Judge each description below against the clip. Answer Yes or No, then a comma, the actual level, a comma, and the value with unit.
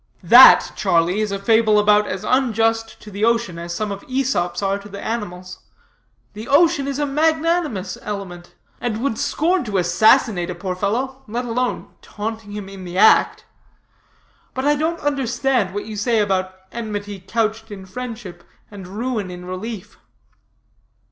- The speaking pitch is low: No, high, 215 Hz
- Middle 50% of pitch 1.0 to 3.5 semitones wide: No, average, 4.3 semitones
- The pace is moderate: Yes, average, 160 wpm